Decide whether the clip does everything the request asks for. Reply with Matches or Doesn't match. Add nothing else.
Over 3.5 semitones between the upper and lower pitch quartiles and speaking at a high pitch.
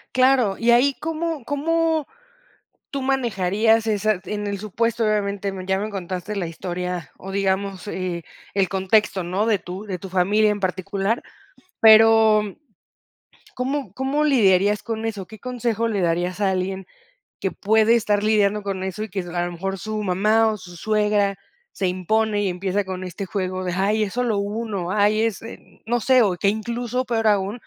Doesn't match